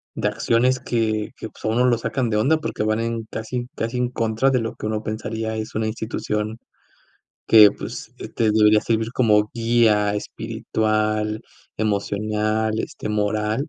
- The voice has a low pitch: Yes, low, 110 Hz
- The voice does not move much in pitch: Yes, narrow, 1.3 semitones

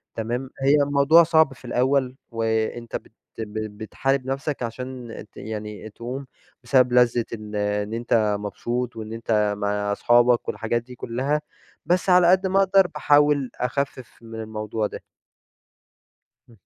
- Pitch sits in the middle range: No, low, 120 Hz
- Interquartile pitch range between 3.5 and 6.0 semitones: Yes, average, 3.9 semitones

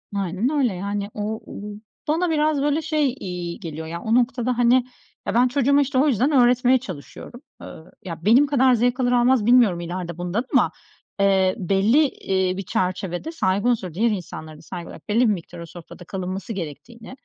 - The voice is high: Yes, high, 220 Hz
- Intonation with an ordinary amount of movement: No, wide, 5.8 semitones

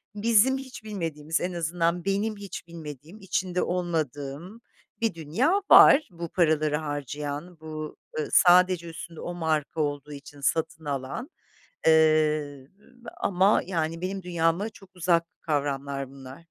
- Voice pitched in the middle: Yes, medium, 165 Hz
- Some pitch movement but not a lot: Yes, average, 3.6 semitones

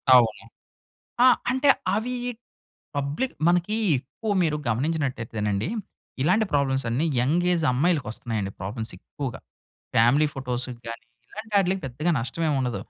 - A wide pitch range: Yes, wide, 6.7 semitones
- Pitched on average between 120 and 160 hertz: Yes, medium, 140 Hz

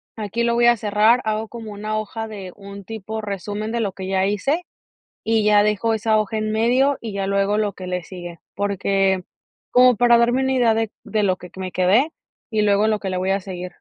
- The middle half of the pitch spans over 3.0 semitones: No, narrow, 2.5 semitones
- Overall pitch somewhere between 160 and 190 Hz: No, high, 210 Hz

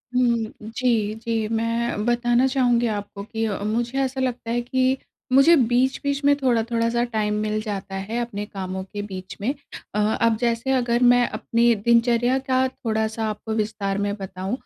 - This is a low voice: No, high, 230 Hz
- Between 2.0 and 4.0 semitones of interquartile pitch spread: Yes, narrow, 2.5 semitones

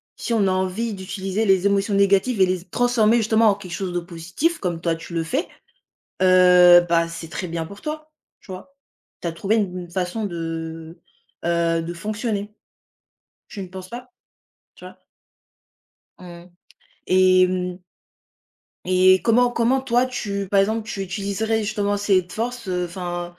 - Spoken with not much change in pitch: No, average, 3.5 semitones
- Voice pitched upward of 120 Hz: Yes, high, 190 Hz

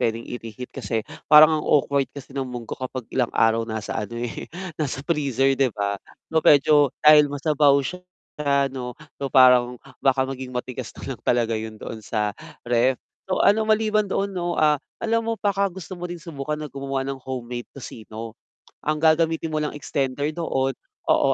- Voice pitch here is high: No, low, 135 Hz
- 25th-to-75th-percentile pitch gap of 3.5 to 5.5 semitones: Yes, average, 3.9 semitones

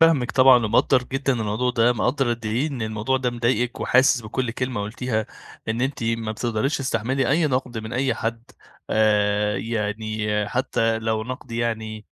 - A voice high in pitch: No, low, 115 Hz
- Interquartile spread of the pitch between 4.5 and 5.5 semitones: No, average, 2.8 semitones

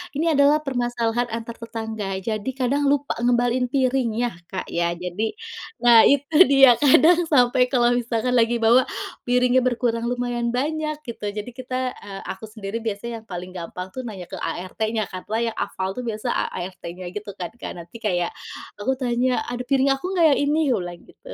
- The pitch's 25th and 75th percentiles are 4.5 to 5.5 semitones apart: No, average, 3.5 semitones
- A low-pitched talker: No, high, 240 Hz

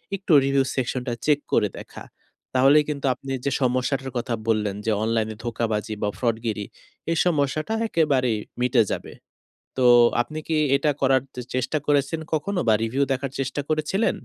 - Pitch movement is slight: No, average, 3.8 semitones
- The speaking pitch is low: Yes, low, 130 Hz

